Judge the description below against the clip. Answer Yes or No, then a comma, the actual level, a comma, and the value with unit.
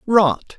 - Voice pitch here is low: No, medium, 185 Hz